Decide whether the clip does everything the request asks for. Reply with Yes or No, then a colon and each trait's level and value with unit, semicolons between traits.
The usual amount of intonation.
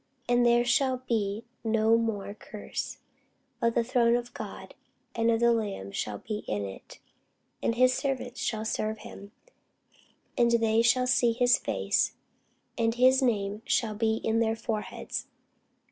No: narrow, 1.9 semitones